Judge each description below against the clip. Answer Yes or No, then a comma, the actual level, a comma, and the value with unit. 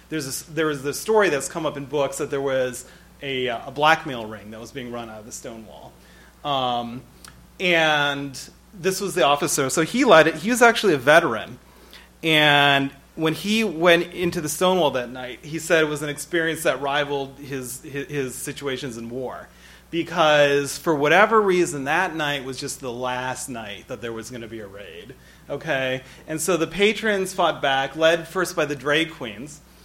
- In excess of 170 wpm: Yes, average, 185 wpm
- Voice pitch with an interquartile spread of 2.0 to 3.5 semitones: No, average, 4.2 semitones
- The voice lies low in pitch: No, medium, 145 Hz